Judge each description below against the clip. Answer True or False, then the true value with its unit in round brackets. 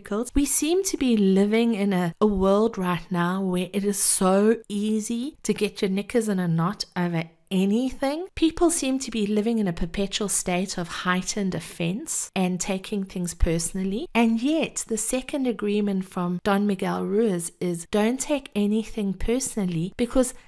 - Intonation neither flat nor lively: True (3.8 semitones)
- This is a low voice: False (205 Hz)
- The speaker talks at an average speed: True (165 wpm)